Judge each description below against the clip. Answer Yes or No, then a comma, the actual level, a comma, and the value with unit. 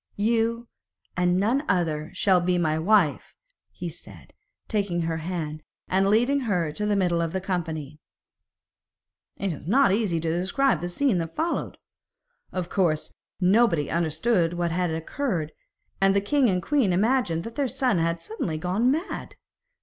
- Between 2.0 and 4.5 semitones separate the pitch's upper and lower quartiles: No, average, 5.1 semitones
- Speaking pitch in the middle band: Yes, medium, 180 Hz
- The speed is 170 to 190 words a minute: No, average, 155 wpm